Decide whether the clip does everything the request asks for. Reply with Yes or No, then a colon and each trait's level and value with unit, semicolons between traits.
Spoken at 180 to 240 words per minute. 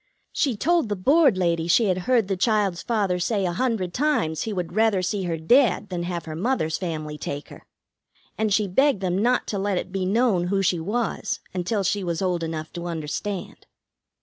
Yes: average, 200 wpm